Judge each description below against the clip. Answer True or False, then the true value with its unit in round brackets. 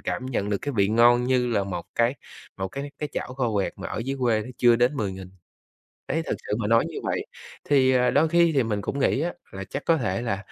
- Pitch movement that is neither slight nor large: True (4.7 semitones)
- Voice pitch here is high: False (120 Hz)